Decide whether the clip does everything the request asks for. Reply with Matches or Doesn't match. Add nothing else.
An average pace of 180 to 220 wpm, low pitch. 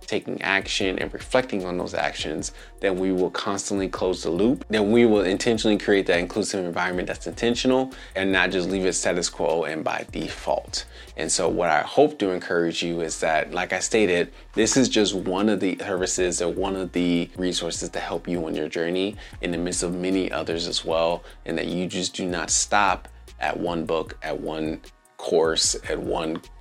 Matches